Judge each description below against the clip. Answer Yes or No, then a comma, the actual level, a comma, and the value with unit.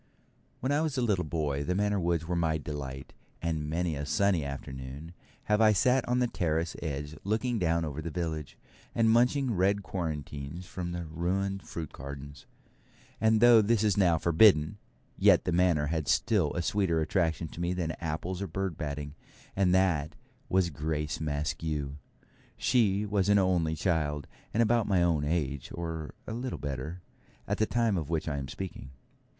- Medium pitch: No, very low, 85 Hz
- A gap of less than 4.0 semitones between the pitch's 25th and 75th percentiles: No, average, 4.7 semitones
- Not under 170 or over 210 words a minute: Yes, average, 175 wpm